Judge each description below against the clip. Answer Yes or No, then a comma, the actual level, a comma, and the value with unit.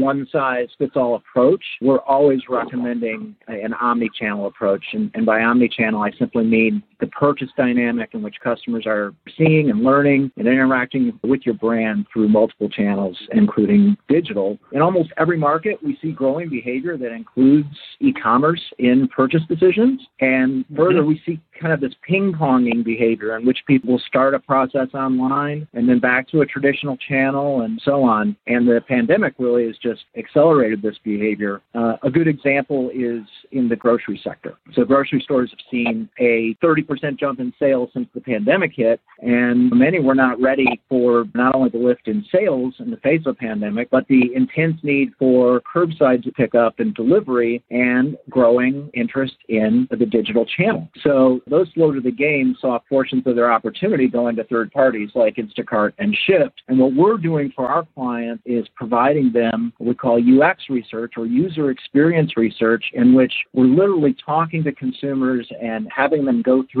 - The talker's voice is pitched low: Yes, low, 130 Hz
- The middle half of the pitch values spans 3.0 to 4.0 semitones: Yes, average, 3.7 semitones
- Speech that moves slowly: No, average, 180 wpm